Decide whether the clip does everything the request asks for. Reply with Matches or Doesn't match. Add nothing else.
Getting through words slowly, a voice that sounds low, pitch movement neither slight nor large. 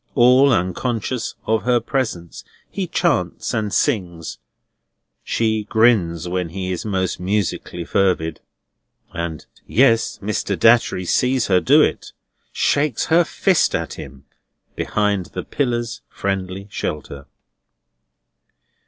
Matches